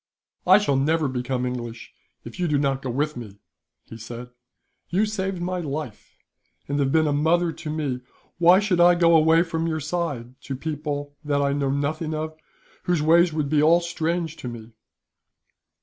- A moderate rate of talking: Yes, average, 180 wpm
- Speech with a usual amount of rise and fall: Yes, average, 3.7 semitones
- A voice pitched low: No, medium, 155 Hz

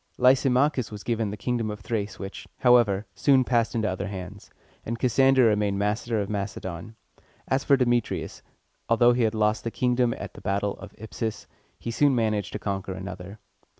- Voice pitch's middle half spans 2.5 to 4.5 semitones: Yes, average, 3.3 semitones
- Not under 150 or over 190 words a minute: Yes, average, 175 wpm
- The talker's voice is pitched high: No, low, 110 Hz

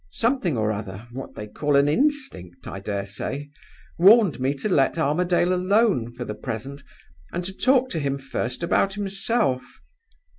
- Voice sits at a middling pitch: Yes, medium, 145 Hz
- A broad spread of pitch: Yes, wide, 8.4 semitones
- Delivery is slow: No, average, 160 wpm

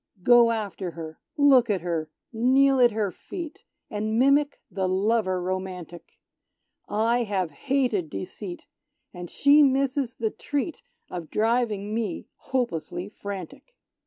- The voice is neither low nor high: No, high, 215 Hz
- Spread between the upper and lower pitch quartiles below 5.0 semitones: No, wide, 5.6 semitones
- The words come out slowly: Yes, slow, 125 wpm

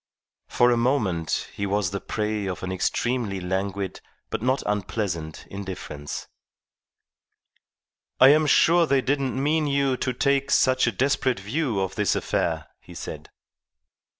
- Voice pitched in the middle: No, low, 110 Hz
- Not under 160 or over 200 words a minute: No, average, 140 wpm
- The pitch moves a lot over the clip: Yes, wide, 5.8 semitones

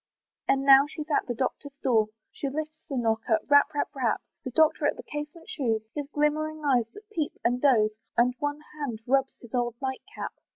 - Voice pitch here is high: Yes, very high, 275 Hz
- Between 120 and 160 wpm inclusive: No, average, 200 wpm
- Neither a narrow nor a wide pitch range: Yes, average, 3.5 semitones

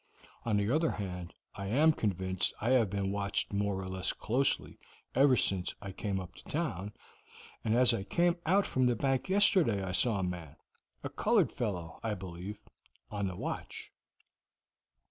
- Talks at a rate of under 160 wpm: No, average, 170 wpm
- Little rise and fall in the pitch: No, average, 5.0 semitones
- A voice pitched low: Yes, low, 100 Hz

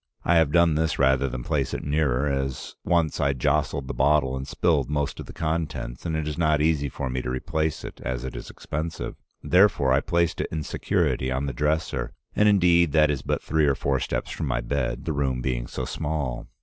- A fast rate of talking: Yes, fast, 220 wpm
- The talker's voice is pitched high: No, very low, 75 Hz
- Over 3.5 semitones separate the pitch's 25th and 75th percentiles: No, average, 3.1 semitones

